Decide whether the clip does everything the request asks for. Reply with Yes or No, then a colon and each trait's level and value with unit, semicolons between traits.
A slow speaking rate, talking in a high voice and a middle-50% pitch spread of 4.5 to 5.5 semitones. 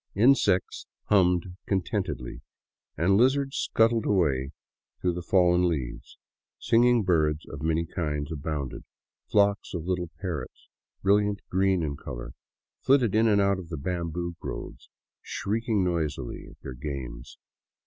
No: slow, 130 wpm; very low, 90 Hz; average, 4.8 semitones